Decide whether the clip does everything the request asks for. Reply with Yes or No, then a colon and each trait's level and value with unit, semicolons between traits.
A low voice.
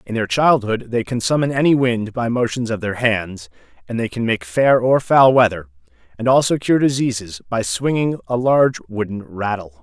Yes: low, 115 Hz